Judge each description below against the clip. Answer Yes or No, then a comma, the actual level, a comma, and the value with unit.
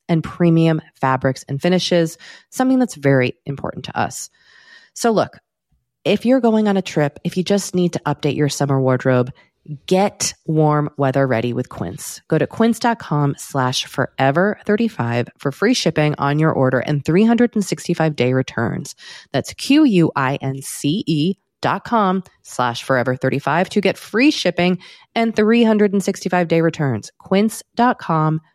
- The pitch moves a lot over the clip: Yes, wide, 6.1 semitones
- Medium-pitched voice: Yes, medium, 160 Hz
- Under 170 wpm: Yes, average, 140 wpm